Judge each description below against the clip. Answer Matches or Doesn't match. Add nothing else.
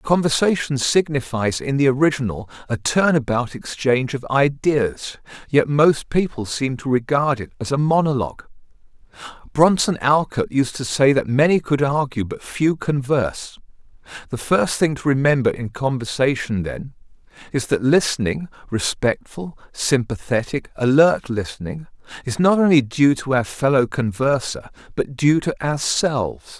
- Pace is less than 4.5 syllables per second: Doesn't match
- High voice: Doesn't match